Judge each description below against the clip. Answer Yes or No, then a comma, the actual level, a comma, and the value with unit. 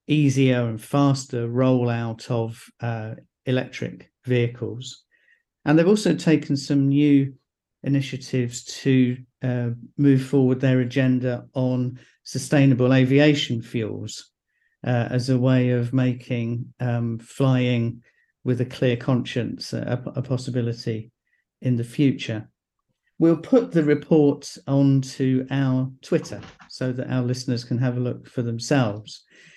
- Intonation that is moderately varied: No, narrow, 2.1 semitones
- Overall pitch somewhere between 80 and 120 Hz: No, low, 130 Hz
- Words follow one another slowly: Yes, slow, 120 wpm